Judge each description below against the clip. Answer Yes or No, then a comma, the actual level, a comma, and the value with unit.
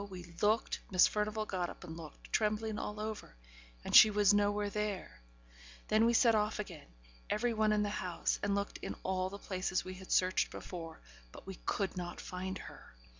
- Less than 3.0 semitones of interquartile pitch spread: Yes, narrow, 2.4 semitones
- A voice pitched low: No, high, 205 Hz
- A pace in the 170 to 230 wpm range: Yes, average, 190 wpm